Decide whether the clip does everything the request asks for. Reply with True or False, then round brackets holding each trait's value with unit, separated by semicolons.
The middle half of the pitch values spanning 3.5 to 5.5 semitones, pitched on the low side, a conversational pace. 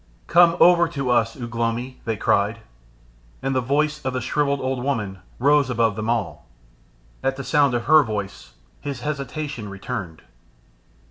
True (3.9 semitones; 125 Hz; 155 wpm)